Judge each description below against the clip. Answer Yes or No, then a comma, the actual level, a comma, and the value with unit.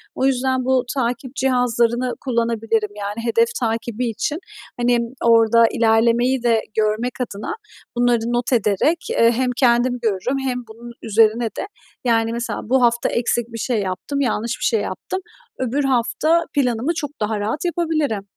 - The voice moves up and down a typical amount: No, narrow, 2.2 semitones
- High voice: Yes, high, 235 Hz